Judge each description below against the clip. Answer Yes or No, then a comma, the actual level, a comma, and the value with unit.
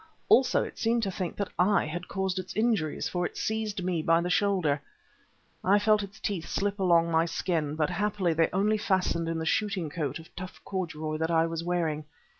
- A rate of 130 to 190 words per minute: No, fast, 205 wpm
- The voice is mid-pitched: Yes, medium, 180 Hz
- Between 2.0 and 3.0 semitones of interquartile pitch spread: No, average, 3.4 semitones